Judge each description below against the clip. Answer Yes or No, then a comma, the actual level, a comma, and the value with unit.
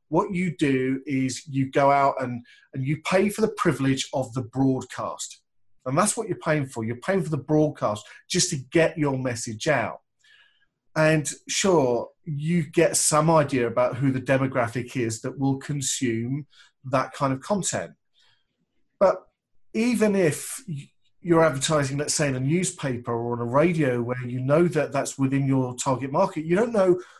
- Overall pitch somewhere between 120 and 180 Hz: Yes, medium, 140 Hz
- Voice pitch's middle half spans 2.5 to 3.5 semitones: No, average, 4.1 semitones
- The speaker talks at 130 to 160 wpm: No, average, 170 wpm